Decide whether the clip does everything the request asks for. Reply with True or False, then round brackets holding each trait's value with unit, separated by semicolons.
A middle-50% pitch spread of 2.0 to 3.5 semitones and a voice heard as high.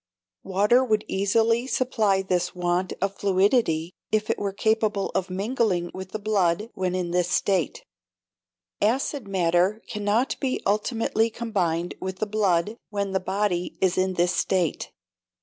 True (3.0 semitones; 195 Hz)